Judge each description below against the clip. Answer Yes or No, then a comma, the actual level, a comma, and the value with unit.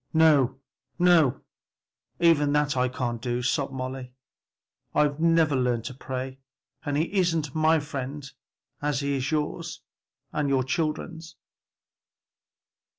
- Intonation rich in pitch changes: No, average, 3.3 semitones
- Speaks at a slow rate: Yes, slow, 120 wpm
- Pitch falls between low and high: Yes, medium, 145 Hz